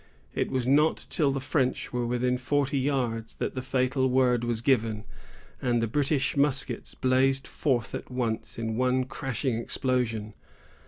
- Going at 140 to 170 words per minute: Yes, average, 155 wpm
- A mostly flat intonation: Yes, narrow, 2.1 semitones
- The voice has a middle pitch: No, low, 130 Hz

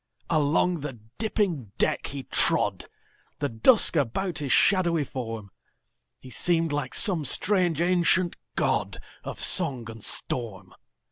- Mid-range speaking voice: Yes, medium, 150 Hz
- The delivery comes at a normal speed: No, slow, 110 wpm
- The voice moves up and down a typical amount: No, wide, 6.2 semitones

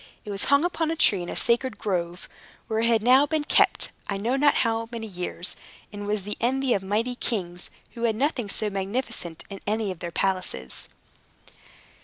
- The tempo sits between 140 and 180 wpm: No, average, 195 wpm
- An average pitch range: Yes, average, 4.3 semitones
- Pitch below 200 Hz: No, high, 220 Hz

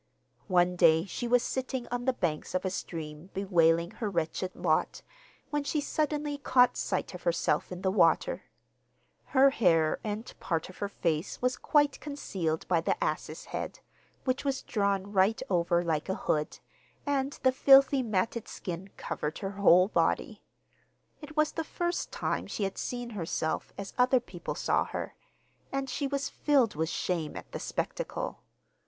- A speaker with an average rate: Yes, average, 165 wpm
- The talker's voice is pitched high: Yes, high, 205 Hz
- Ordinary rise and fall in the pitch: No, wide, 7.5 semitones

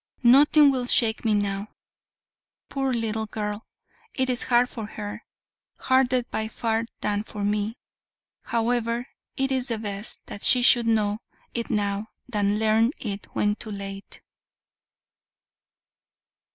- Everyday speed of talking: No, slow, 125 wpm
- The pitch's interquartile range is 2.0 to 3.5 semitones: Yes, average, 2.8 semitones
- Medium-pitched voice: No, high, 220 Hz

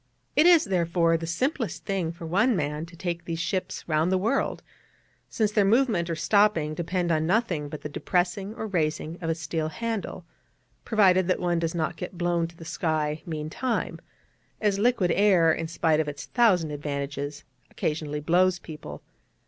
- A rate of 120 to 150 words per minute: No, average, 175 wpm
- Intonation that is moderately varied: Yes, average, 3.7 semitones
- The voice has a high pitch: No, medium, 170 Hz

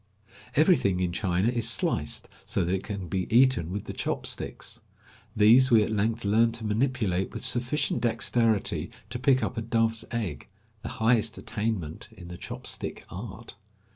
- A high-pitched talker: No, low, 110 Hz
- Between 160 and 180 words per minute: Yes, average, 170 wpm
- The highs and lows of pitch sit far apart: No, average, 3.4 semitones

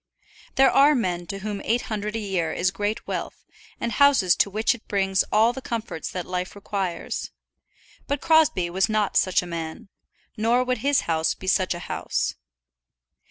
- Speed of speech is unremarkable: Yes, average, 175 wpm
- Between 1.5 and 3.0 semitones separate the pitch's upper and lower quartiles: No, average, 4.3 semitones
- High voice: Yes, high, 205 Hz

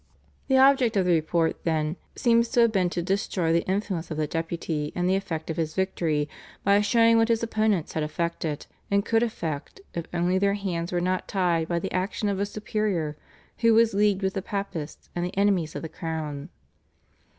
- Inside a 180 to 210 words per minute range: Yes, average, 200 wpm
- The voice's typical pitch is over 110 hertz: Yes, medium, 185 Hz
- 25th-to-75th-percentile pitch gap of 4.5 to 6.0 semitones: No, average, 3.9 semitones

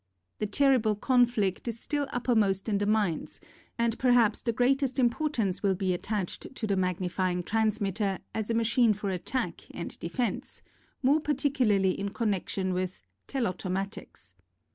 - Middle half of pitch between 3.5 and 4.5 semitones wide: Yes, average, 4.2 semitones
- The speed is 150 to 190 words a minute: No, average, 140 wpm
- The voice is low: No, high, 215 Hz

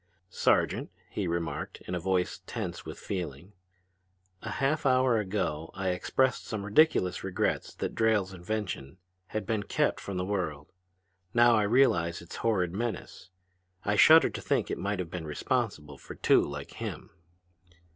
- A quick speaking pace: No, average, 155 wpm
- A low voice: Yes, very low, 95 Hz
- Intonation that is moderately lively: Yes, average, 4.1 semitones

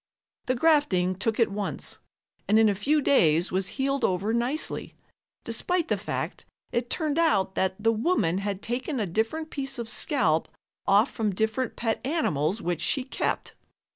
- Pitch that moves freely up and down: Yes, wide, 6.2 semitones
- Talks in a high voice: Yes, high, 225 Hz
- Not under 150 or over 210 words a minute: Yes, average, 165 wpm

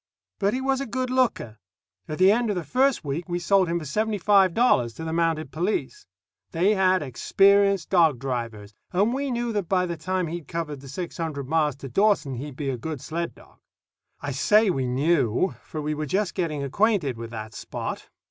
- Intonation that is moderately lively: No, wide, 6.1 semitones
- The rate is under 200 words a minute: No, fast, 205 wpm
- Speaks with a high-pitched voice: No, medium, 170 Hz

